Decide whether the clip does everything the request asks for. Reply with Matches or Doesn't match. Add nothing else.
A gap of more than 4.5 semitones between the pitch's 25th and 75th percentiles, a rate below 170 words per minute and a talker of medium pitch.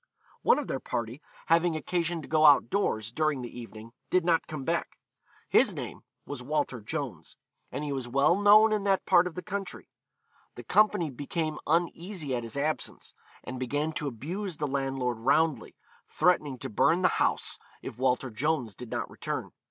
Doesn't match